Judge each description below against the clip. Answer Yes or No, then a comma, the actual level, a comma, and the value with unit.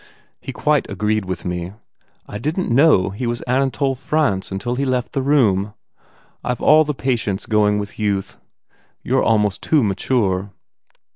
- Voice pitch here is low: Yes, low, 110 Hz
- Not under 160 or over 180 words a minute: Yes, average, 165 wpm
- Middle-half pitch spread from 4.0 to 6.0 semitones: Yes, average, 5.1 semitones